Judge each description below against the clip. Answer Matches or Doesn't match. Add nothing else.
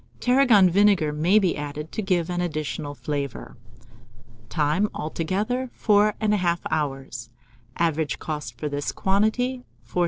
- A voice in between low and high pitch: Matches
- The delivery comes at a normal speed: Doesn't match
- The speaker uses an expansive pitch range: Matches